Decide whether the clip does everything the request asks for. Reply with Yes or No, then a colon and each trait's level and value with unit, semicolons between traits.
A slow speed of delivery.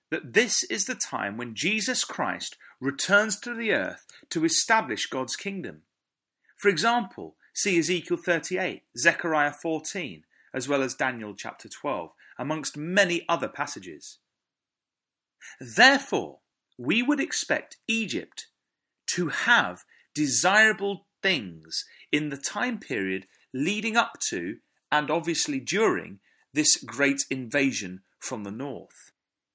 Yes: slow, 120 wpm